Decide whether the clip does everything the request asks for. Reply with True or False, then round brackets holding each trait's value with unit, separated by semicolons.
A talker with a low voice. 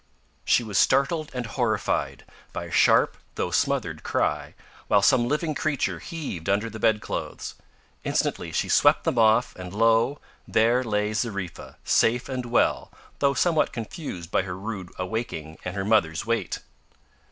True (110 Hz)